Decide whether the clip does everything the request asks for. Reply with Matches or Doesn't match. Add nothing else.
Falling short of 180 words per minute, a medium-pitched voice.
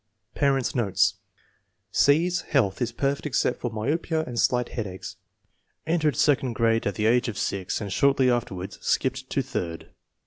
Doesn't match